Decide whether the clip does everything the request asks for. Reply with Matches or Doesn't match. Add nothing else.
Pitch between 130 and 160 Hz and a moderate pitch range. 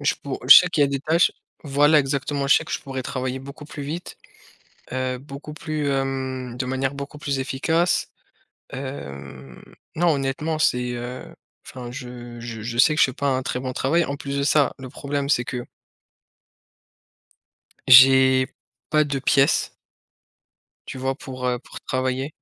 Doesn't match